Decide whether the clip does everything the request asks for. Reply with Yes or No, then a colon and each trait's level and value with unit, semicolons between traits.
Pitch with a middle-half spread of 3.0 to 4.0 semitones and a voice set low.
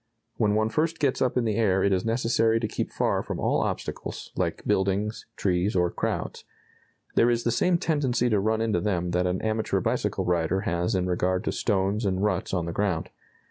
Yes: average, 3.7 semitones; low, 105 Hz